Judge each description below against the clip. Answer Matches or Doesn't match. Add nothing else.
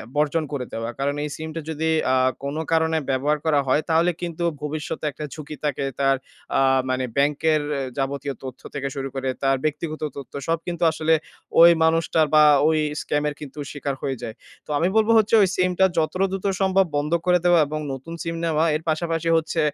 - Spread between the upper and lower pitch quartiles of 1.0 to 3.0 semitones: Matches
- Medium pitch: Matches